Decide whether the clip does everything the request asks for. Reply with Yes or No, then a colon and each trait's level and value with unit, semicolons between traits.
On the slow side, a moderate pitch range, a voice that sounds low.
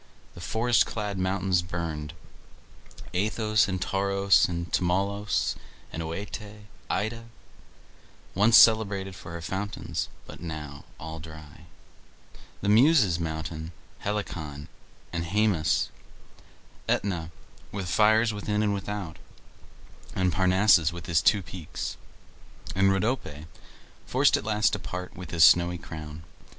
Yes: slow, 115 wpm; average, 3.8 semitones; very low, 95 Hz